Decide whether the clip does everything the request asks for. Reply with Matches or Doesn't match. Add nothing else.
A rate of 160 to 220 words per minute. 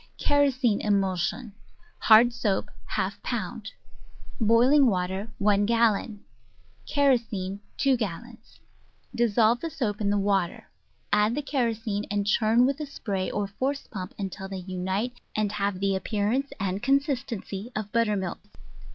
Doesn't match